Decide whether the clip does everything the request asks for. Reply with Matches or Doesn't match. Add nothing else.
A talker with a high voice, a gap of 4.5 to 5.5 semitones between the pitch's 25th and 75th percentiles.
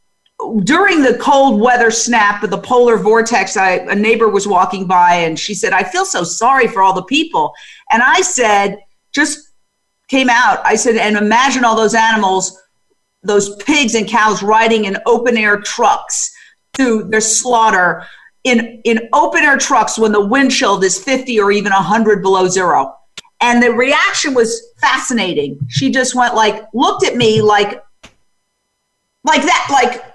Doesn't match